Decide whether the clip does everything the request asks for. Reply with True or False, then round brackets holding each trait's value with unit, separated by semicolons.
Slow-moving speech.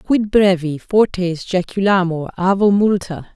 True (105 wpm)